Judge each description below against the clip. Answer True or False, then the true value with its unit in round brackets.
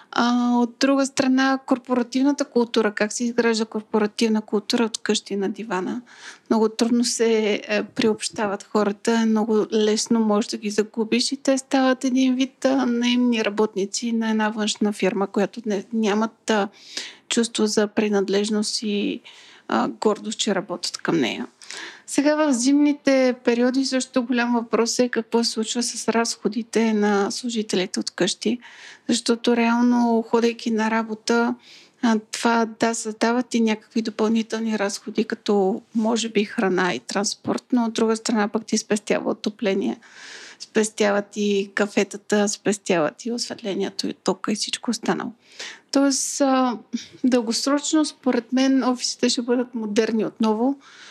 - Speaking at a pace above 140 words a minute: False (130 wpm)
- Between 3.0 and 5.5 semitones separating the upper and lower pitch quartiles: False (2.5 semitones)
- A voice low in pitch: False (225 Hz)